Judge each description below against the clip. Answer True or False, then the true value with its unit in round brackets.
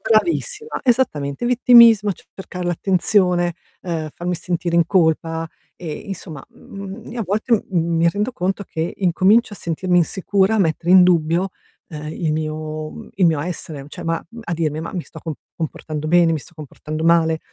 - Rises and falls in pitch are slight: False (3.4 semitones)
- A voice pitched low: False (175 Hz)